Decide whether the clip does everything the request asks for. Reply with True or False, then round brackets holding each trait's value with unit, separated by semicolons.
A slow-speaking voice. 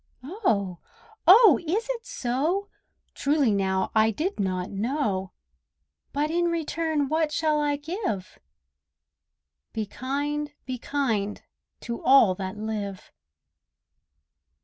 True (105 wpm)